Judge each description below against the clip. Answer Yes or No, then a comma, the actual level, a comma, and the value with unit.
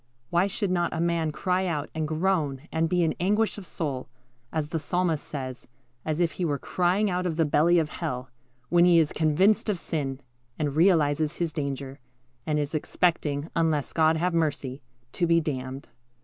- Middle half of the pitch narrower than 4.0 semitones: Yes, average, 3.0 semitones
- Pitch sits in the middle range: Yes, medium, 160 Hz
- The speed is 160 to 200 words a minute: Yes, average, 185 wpm